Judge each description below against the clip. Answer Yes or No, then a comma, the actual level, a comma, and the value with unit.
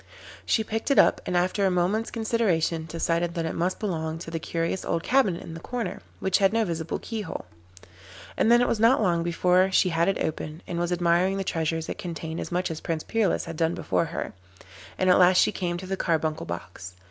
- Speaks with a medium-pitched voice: Yes, medium, 175 Hz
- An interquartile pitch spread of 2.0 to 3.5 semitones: Yes, average, 2.8 semitones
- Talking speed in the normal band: No, fast, 220 wpm